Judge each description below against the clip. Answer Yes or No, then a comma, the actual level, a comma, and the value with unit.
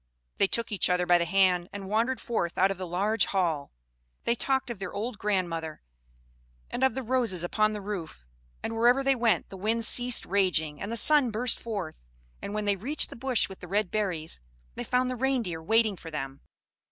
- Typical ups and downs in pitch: Yes, average, 4.6 semitones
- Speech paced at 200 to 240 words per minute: Yes, fast, 205 wpm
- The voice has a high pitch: Yes, high, 205 Hz